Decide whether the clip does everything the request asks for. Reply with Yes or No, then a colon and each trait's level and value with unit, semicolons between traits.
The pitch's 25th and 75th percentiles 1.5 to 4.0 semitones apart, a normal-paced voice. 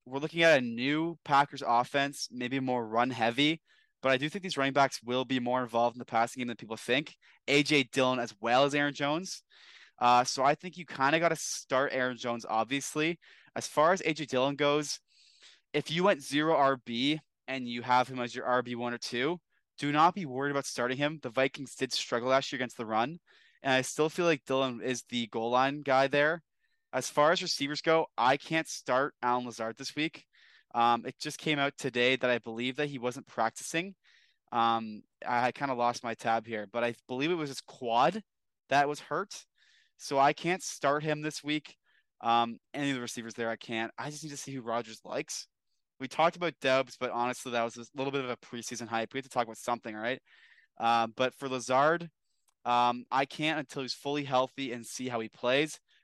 No: average, 3.5 semitones; fast, 215 wpm